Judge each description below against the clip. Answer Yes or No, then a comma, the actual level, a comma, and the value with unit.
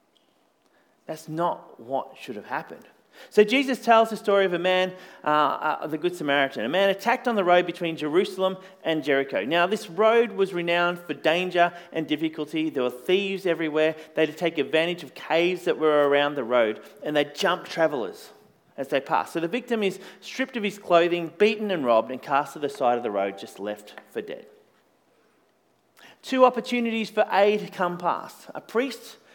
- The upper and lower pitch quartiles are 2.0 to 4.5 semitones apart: No, average, 4.9 semitones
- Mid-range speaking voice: Yes, medium, 175 Hz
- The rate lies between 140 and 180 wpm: No, average, 190 wpm